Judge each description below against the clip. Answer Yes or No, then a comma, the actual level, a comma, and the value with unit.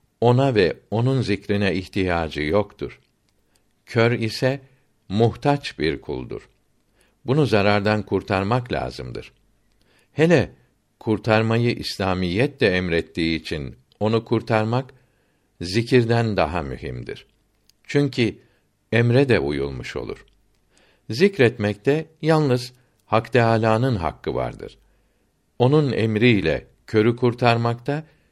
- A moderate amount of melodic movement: Yes, average, 4.4 semitones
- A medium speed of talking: No, slow, 85 wpm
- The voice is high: No, low, 110 Hz